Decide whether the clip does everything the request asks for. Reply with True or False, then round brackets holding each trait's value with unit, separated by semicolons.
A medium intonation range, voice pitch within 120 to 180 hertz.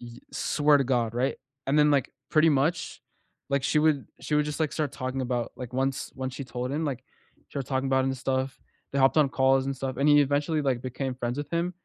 False (2.1 semitones; 135 Hz)